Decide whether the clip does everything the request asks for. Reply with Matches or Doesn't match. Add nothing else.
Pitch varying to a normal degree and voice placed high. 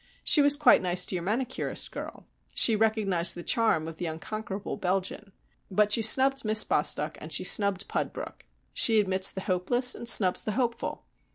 Matches